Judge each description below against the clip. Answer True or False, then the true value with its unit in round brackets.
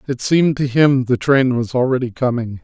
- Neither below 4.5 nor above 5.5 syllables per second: True (5.3 syllables/s)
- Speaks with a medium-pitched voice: False (130 Hz)